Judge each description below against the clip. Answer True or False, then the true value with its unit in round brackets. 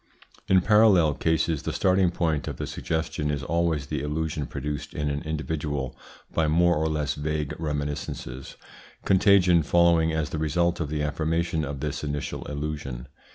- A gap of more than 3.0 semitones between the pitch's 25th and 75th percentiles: False (2.4 semitones)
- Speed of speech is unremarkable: True (155 wpm)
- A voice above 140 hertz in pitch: False (75 Hz)